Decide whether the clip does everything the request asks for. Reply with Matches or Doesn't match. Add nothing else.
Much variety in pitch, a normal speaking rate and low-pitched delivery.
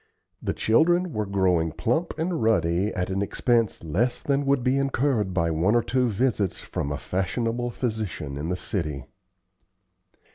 Matches